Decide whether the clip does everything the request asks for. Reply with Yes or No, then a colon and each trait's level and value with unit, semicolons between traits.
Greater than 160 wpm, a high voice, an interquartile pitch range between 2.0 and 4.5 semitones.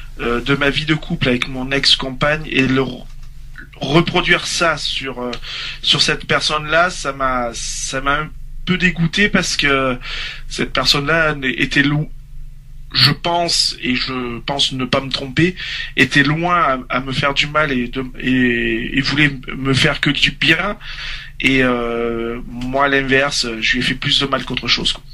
No: average, 180 wpm; medium, 140 Hz; average, 2.9 semitones